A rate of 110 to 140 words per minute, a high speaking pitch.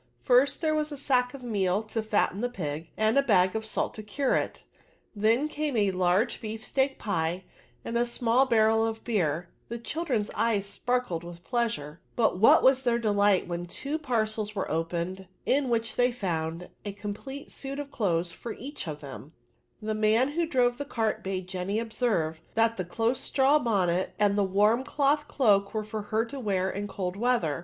No: average, 190 wpm; high, 220 Hz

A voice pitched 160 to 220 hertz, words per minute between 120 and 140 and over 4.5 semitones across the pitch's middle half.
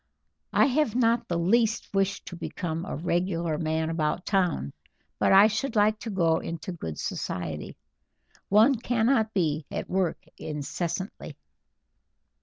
Yes: medium, 185 Hz; slow, 135 wpm; average, 5.1 semitones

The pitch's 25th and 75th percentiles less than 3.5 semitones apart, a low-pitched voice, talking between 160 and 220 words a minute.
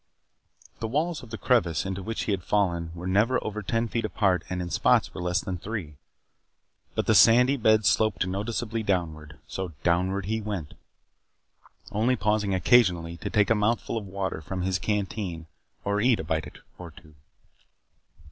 No: average, 3.8 semitones; low, 100 Hz; average, 170 wpm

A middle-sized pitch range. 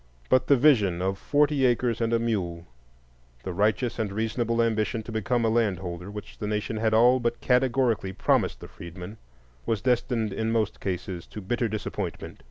Yes: average, 4.2 semitones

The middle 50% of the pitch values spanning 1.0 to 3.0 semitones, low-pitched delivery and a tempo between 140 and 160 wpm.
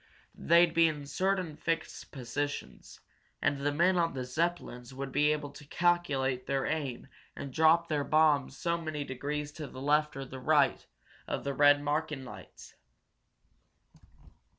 No: average, 2.7 semitones; medium, 145 Hz; average, 150 wpm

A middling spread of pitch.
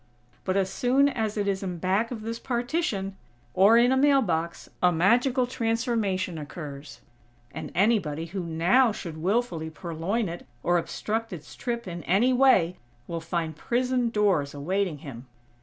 No: wide, 5.9 semitones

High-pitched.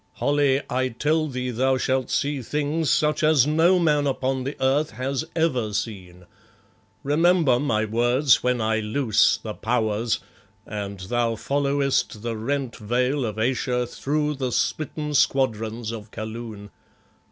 No: low, 130 Hz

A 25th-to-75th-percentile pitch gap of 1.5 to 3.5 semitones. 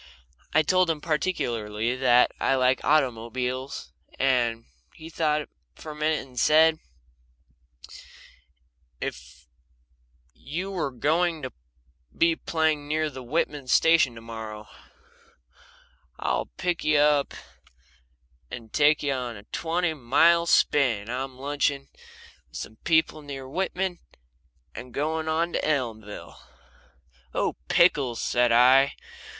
No: average, 4.3 semitones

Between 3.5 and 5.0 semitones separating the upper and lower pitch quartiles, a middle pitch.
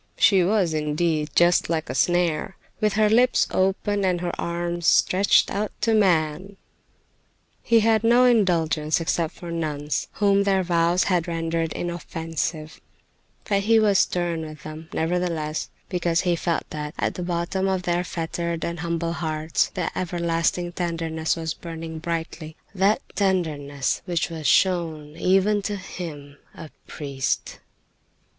No: average, 2.8 semitones; medium, 170 Hz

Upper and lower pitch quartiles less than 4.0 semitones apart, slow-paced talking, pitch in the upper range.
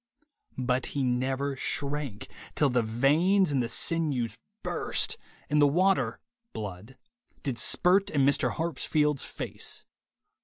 No: average, 3.4 semitones; slow, 120 wpm; medium, 140 Hz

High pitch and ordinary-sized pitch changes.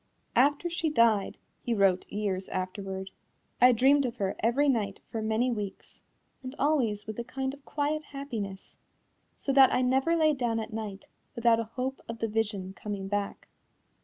Yes: high, 230 Hz; average, 4.7 semitones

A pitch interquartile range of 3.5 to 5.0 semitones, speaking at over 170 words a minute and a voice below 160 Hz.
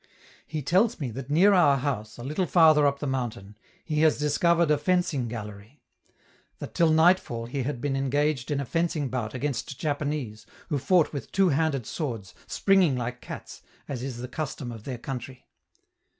Yes: average, 4.2 semitones; average, 180 wpm; medium, 140 Hz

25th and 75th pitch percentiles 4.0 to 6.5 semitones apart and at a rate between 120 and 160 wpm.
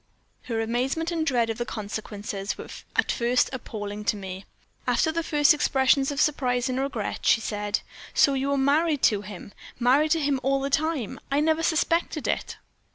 No: average, 5.1 semitones; average, 180 wpm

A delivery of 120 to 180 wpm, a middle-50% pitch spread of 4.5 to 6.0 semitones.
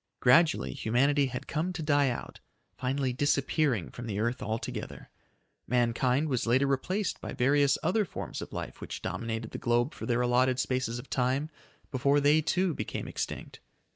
No: average, 165 wpm; average, 3.1 semitones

